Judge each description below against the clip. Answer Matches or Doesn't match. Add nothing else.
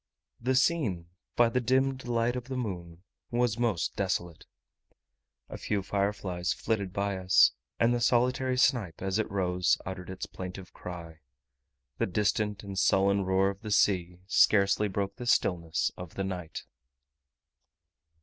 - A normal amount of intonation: Matches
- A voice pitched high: Doesn't match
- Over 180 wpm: Doesn't match